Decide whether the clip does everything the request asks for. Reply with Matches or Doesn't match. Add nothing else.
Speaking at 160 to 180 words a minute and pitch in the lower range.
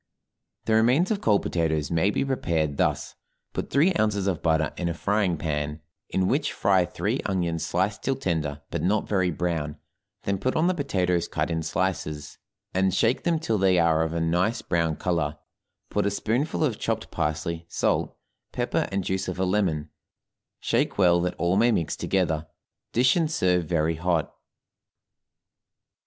Matches